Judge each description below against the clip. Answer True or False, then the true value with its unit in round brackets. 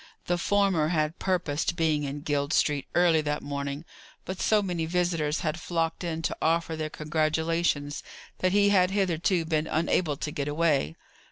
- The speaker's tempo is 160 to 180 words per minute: True (165 wpm)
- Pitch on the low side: False (160 Hz)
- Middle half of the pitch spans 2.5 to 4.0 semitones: True (2.8 semitones)